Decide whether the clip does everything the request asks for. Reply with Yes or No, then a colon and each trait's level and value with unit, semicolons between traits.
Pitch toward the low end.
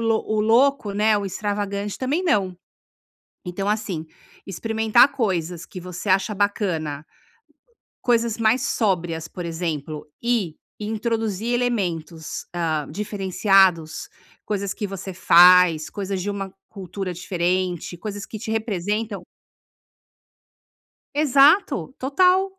No: high, 200 Hz